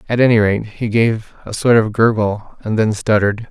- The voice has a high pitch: No, low, 110 Hz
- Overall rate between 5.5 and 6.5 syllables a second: No, 5.1 syllables/s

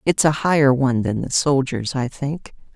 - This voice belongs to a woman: Yes, female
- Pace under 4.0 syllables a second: No, 4.9 syllables/s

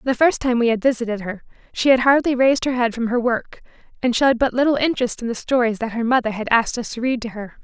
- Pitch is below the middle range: No, high, 240 Hz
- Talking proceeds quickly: Yes, fast, 265 wpm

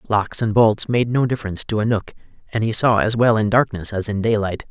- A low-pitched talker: Yes, low, 110 Hz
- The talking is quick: Yes, fast, 240 wpm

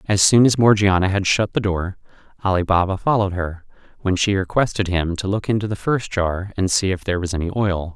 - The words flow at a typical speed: No, fast, 220 wpm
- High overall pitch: No, very low, 95 Hz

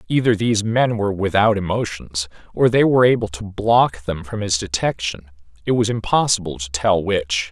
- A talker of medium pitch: No, low, 100 Hz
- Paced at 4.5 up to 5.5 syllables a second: Yes, 5.2 syllables/s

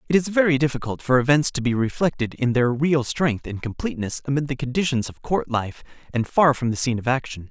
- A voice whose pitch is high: No, low, 130 Hz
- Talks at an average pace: No, fast, 225 wpm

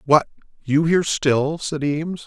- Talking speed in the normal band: Yes, average, 160 wpm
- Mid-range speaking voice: Yes, medium, 150 Hz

